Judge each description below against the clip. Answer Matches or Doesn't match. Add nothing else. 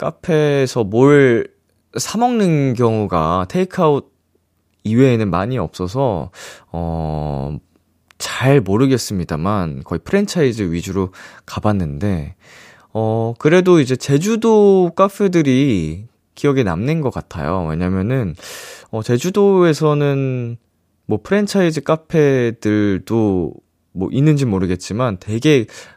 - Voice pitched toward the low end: Matches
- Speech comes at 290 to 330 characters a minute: Doesn't match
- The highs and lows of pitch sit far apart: Matches